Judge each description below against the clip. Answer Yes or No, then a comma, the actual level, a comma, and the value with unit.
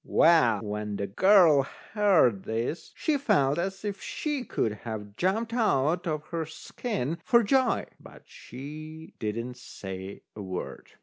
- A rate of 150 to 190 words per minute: No, average, 140 wpm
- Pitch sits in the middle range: Yes, medium, 155 Hz